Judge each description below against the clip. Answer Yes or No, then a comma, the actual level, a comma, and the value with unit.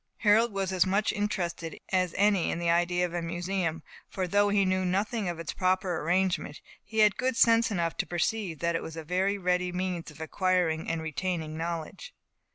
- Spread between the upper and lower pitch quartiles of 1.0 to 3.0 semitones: Yes, average, 2.7 semitones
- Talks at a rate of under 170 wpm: No, average, 195 wpm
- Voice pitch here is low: No, medium, 180 Hz